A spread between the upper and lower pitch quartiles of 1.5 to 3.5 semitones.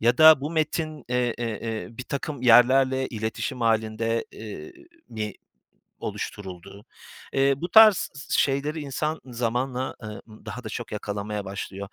No: average, 4.1 semitones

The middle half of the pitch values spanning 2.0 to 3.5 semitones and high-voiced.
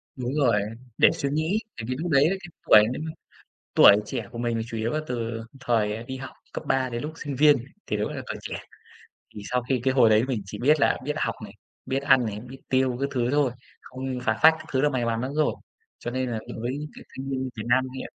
No: average, 2.9 semitones; low, 130 Hz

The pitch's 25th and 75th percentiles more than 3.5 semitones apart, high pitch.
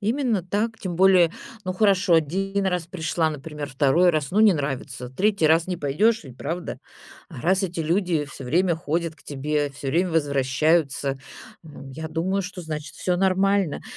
No: average, 4.3 semitones; medium, 165 Hz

